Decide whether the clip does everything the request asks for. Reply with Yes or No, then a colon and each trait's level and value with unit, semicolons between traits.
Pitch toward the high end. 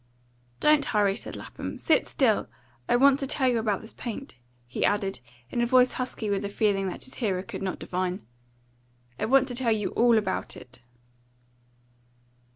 Yes: high, 220 Hz